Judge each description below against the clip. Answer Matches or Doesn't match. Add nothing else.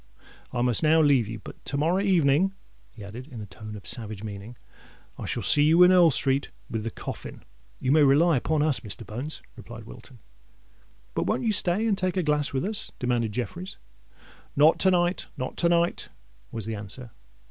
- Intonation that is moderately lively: Doesn't match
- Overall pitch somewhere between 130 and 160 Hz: Matches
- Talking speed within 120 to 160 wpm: Doesn't match